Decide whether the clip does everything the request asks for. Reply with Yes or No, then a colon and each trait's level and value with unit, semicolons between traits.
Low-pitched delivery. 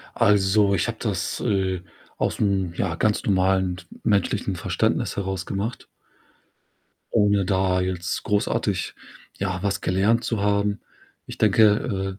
Yes: very low, 95 Hz